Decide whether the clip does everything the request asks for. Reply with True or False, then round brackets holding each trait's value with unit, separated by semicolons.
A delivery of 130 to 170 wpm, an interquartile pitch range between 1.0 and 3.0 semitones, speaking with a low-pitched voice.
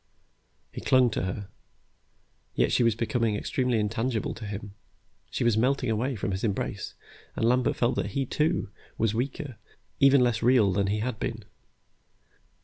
False (160 wpm; 3.4 semitones; 115 Hz)